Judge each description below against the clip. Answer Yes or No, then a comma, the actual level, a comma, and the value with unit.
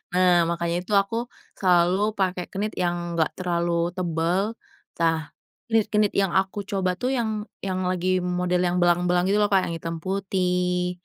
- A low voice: No, medium, 180 Hz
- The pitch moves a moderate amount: No, narrow, 2.2 semitones